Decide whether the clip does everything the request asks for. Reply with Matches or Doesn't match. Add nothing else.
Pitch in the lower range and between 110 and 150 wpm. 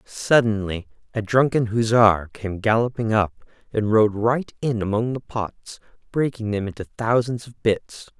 Matches